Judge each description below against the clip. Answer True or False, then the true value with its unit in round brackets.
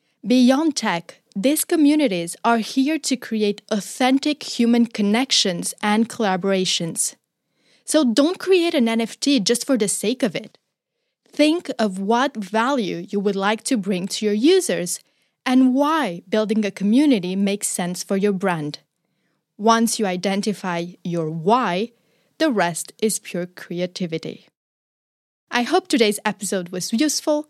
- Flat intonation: False (5.6 semitones)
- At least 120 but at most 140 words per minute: True (135 wpm)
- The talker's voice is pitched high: True (220 Hz)